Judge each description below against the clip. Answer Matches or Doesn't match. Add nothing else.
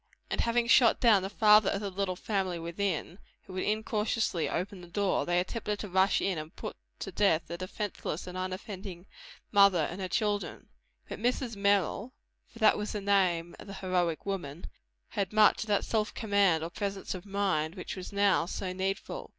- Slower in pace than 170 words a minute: Doesn't match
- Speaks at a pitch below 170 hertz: Doesn't match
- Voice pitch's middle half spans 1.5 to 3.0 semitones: Matches